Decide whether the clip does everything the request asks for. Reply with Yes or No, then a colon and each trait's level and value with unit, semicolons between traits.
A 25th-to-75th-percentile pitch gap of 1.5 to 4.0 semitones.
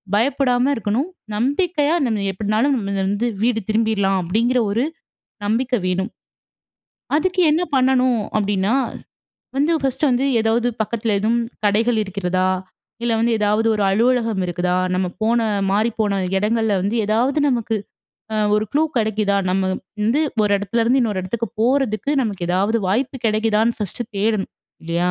Yes: average, 3.3 semitones